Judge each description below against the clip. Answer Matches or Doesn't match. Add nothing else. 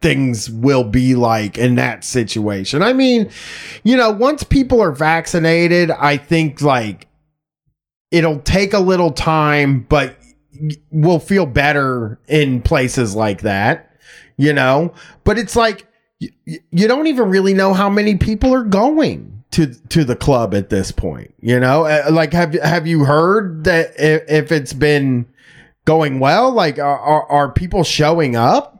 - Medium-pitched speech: Matches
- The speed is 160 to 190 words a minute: Doesn't match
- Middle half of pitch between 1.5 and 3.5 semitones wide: Doesn't match